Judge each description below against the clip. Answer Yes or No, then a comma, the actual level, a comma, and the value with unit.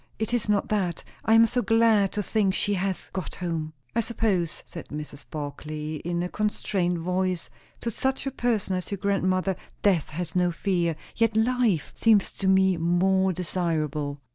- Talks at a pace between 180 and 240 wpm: No, average, 170 wpm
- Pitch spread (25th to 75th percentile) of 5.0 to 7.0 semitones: No, average, 3.8 semitones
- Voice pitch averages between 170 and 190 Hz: Yes, medium, 185 Hz